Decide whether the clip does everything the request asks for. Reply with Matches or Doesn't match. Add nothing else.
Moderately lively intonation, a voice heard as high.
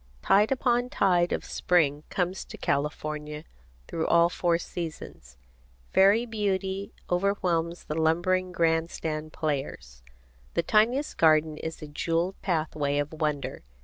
Doesn't match